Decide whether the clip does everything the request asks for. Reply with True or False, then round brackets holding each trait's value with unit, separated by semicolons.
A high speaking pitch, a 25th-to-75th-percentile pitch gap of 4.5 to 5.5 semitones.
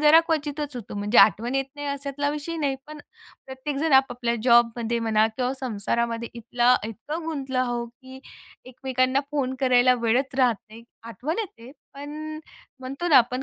False (255 Hz; 3.2 semitones)